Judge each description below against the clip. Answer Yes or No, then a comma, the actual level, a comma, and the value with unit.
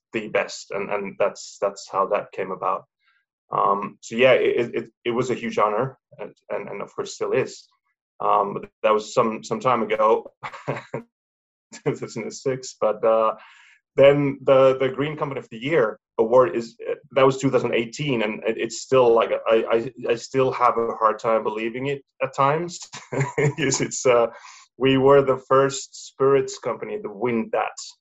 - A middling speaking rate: Yes, average, 170 wpm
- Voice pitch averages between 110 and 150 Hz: Yes, medium, 140 Hz